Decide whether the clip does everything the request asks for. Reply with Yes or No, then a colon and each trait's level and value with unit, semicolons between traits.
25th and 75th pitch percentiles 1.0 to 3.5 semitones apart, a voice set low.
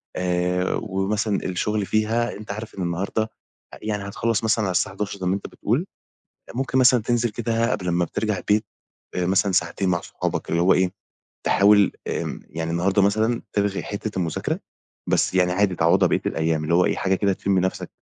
Yes: average, 3.0 semitones; low, 100 Hz